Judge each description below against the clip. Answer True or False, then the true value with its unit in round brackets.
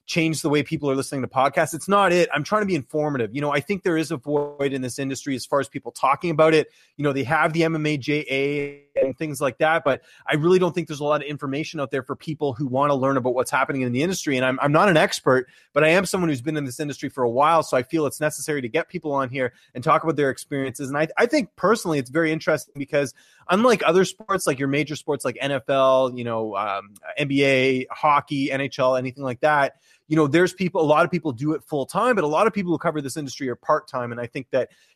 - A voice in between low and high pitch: True (145 Hz)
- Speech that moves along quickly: True (270 wpm)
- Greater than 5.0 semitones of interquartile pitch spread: False (2.8 semitones)